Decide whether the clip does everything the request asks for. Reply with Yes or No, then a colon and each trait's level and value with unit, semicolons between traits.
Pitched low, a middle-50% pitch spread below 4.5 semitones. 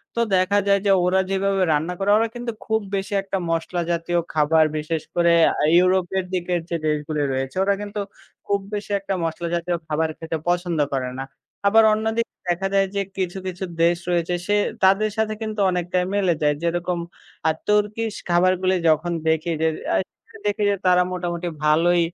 No: medium, 180 Hz; average, 2.9 semitones